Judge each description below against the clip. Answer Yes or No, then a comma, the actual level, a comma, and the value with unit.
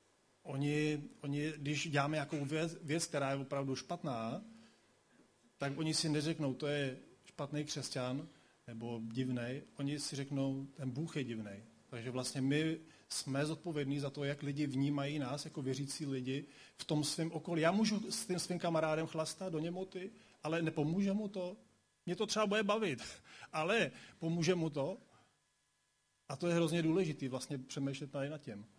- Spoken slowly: No, average, 165 wpm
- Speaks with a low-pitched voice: No, medium, 150 Hz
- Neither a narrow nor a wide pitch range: Yes, average, 3.1 semitones